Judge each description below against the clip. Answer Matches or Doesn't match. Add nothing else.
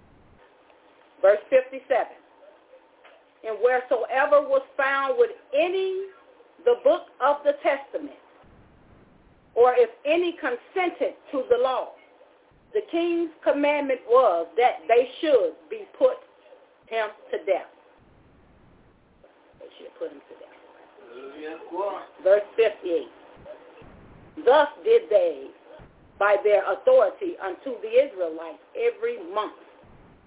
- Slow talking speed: Matches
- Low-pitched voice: Doesn't match